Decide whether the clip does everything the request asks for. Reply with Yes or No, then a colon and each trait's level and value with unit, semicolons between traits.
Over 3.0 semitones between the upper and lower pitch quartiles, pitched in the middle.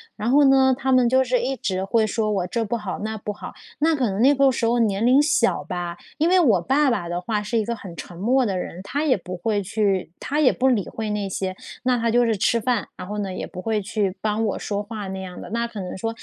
No: average, 4.4 semitones; high, 220 Hz